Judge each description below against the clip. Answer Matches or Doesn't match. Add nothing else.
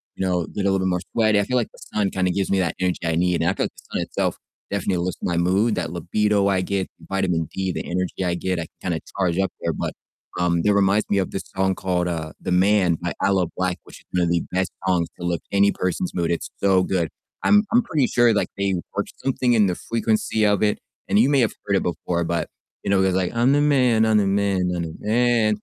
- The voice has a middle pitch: Doesn't match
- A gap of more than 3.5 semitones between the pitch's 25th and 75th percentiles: Doesn't match